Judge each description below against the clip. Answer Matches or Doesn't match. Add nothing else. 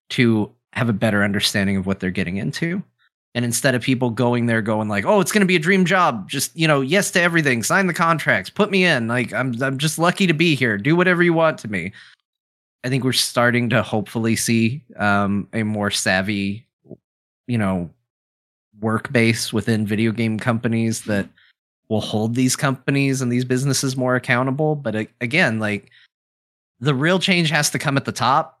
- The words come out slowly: Doesn't match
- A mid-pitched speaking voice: Doesn't match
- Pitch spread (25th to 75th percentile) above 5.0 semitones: Matches